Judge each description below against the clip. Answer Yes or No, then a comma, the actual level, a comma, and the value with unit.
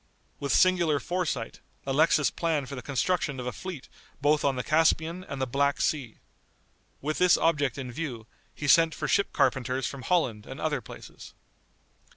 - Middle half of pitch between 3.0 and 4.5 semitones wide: Yes, average, 3.7 semitones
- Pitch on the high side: No, medium, 145 Hz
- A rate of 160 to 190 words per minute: Yes, average, 170 wpm